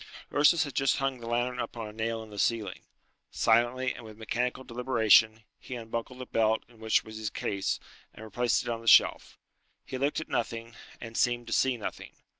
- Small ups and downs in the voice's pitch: Yes, narrow, 2.0 semitones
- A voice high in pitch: No, low, 115 Hz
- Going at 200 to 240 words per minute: Yes, fast, 205 wpm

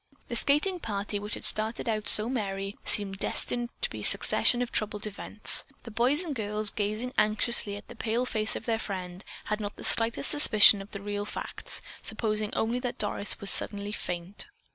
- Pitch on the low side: No, high, 215 Hz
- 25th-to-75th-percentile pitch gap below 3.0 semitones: Yes, narrow, 2.5 semitones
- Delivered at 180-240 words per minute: Yes, average, 190 wpm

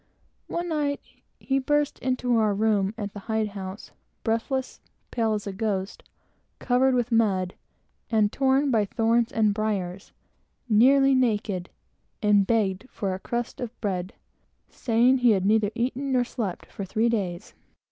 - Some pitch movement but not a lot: Yes, average, 3.7 semitones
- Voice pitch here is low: No, high, 225 Hz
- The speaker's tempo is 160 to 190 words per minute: No, average, 145 wpm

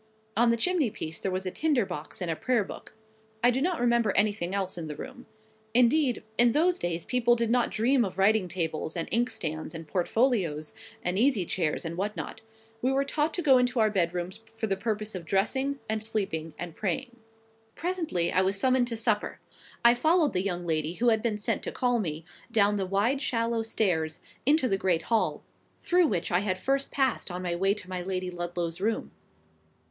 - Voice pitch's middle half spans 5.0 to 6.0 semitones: Yes, wide, 5.5 semitones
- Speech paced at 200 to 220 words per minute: Yes, fast, 205 wpm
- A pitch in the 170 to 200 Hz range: No, high, 210 Hz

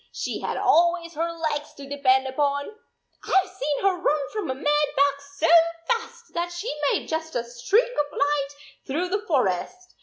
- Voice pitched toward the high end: Yes, very high, 300 Hz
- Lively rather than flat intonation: No, average, 4.1 semitones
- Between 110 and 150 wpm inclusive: No, average, 180 wpm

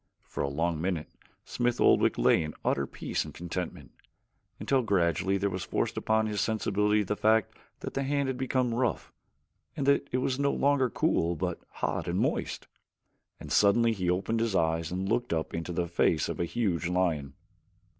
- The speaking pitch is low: Yes, low, 100 Hz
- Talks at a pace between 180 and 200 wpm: Yes, average, 185 wpm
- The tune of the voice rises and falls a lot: Yes, wide, 5.7 semitones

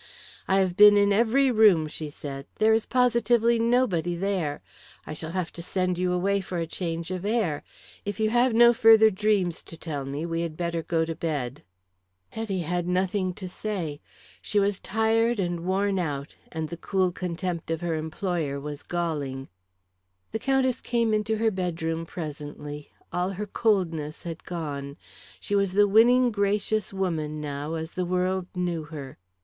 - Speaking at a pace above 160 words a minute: Yes, average, 170 wpm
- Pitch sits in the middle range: Yes, medium, 180 Hz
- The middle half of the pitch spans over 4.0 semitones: Yes, average, 4.4 semitones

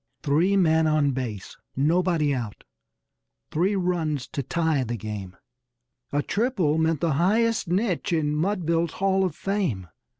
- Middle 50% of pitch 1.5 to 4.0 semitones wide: No, average, 4.6 semitones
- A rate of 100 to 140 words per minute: Yes, slow, 135 wpm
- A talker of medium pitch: Yes, medium, 160 Hz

